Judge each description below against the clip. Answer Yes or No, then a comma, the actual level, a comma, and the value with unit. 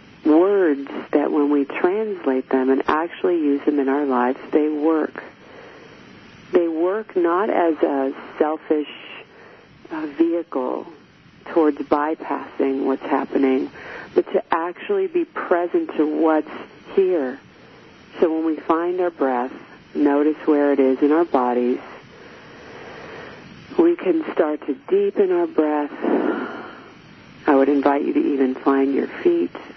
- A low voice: No, medium, 155 Hz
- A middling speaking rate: No, slow, 125 wpm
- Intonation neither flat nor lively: No, wide, 7.4 semitones